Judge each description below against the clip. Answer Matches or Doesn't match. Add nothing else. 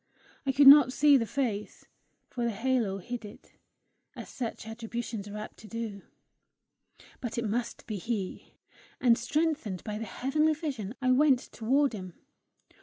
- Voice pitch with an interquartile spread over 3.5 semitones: Matches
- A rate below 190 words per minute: Matches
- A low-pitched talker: Doesn't match